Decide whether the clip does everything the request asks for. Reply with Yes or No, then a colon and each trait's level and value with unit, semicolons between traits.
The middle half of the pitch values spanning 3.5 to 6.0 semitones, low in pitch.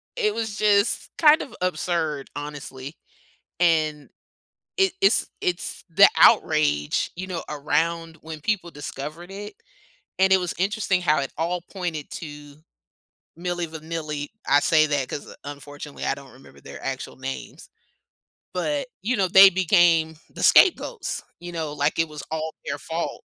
No: average, 4.1 semitones; medium, 165 Hz